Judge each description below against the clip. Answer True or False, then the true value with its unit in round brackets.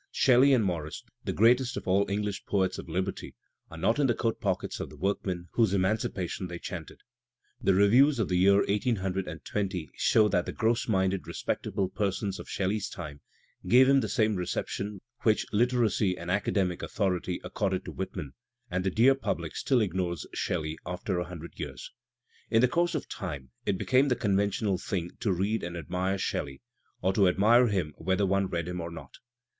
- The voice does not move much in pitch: False (3.5 semitones)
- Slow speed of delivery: False (180 wpm)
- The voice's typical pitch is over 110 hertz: False (95 Hz)